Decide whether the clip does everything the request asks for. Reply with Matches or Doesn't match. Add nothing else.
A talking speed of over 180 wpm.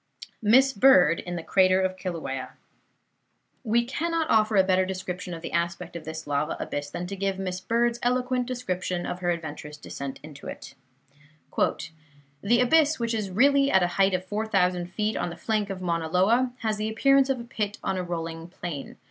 Matches